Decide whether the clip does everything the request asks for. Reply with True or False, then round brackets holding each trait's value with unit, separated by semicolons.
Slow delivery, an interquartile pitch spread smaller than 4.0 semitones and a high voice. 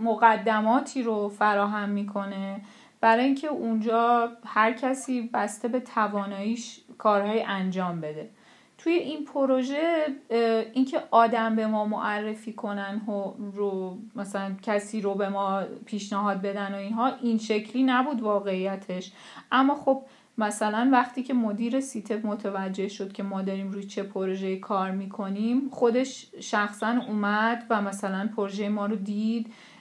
True (130 wpm; 2.8 semitones; 215 Hz)